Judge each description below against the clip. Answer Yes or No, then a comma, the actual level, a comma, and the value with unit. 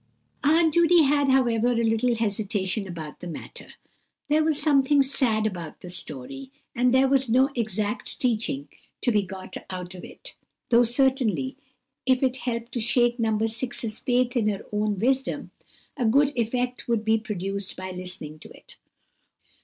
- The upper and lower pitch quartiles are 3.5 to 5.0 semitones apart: Yes, average, 4.1 semitones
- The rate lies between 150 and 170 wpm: Yes, average, 160 wpm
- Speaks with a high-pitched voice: Yes, high, 235 Hz